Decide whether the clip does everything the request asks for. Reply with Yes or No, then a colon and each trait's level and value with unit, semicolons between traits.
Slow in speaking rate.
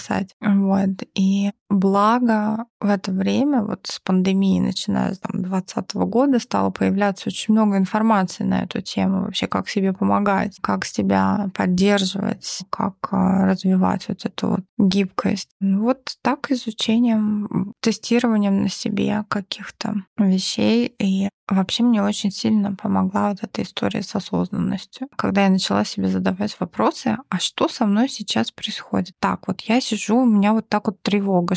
No: average, 145 wpm